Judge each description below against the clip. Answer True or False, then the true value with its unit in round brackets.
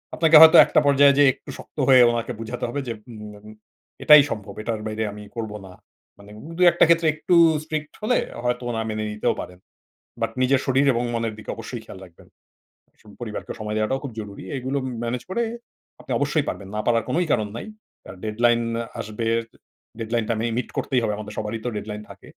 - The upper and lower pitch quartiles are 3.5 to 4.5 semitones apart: True (3.8 semitones)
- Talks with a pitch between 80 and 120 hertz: True (115 Hz)